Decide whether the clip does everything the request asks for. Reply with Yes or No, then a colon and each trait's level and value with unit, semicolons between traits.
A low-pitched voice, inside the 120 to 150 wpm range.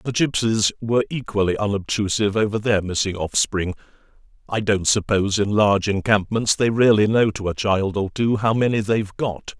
No: low, 105 Hz; average, 170 wpm